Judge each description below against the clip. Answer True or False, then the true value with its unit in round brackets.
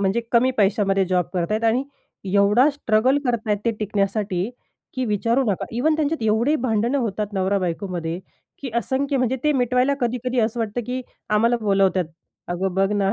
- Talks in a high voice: True (220 Hz)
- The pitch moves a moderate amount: True (4.2 semitones)